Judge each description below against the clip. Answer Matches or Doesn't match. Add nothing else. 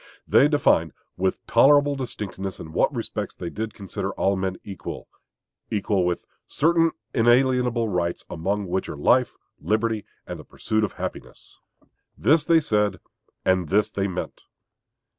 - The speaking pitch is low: Matches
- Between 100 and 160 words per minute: Matches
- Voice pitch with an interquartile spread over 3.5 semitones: Matches